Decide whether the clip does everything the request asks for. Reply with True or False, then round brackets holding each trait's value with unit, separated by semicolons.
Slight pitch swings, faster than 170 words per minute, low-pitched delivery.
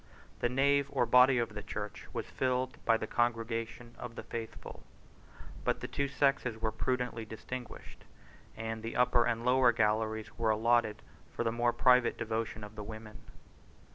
False (2.1 semitones; 165 wpm; 115 Hz)